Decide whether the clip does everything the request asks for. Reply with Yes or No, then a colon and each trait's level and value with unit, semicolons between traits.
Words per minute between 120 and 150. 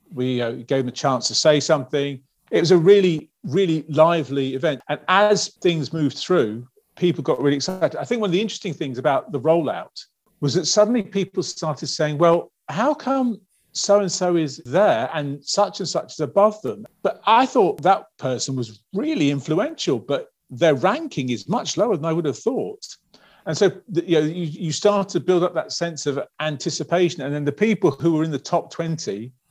No: average, 200 wpm